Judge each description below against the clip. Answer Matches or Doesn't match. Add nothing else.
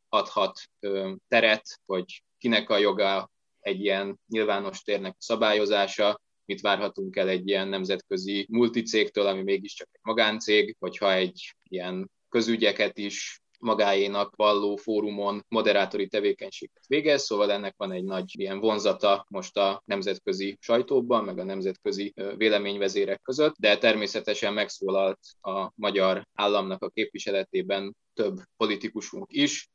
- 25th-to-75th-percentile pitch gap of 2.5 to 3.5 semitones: Doesn't match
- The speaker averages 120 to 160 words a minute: Matches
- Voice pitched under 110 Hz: Matches